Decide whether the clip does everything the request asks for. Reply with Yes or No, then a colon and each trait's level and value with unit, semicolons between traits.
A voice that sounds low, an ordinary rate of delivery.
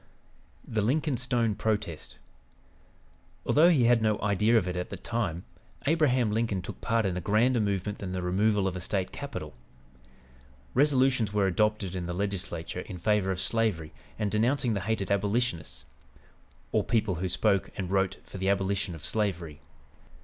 Yes: low, 100 Hz; average, 165 wpm